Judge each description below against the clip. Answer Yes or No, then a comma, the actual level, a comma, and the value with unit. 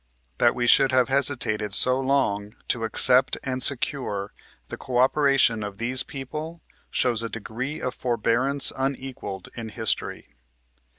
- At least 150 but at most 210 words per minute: No, slow, 135 wpm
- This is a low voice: Yes, low, 125 Hz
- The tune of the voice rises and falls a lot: No, average, 3.1 semitones